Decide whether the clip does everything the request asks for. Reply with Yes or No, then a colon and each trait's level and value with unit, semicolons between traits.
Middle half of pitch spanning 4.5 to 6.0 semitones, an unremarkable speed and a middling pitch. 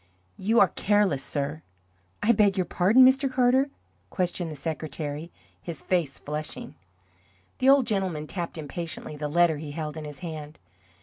Yes: average, 5.2 semitones; average, 150 wpm; medium, 170 Hz